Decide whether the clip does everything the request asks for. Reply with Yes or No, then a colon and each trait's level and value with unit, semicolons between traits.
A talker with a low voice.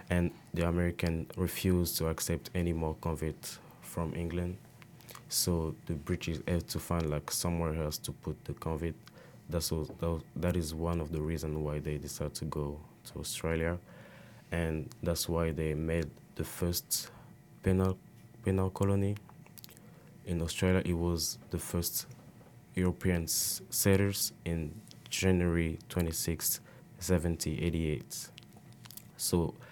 Yes: very low, 85 Hz